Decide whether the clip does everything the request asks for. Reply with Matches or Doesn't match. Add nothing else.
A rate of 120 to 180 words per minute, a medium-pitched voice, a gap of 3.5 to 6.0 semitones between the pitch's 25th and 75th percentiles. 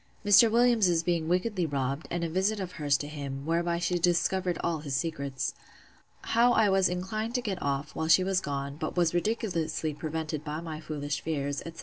Doesn't match